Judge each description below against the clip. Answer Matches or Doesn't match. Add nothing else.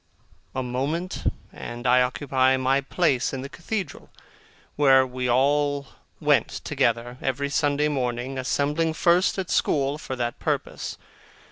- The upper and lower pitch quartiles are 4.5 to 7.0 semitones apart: Doesn't match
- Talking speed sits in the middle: Doesn't match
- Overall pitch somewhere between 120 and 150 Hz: Matches